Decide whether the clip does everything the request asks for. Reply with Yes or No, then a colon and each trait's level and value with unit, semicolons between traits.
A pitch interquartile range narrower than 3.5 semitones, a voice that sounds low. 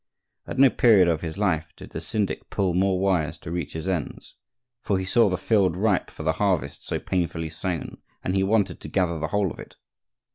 Yes: average, 3.1 semitones; very low, 95 Hz